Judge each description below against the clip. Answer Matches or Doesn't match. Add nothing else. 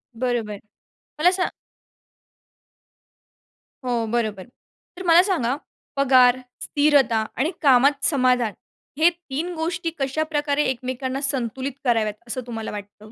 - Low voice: Doesn't match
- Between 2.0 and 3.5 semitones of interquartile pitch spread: Doesn't match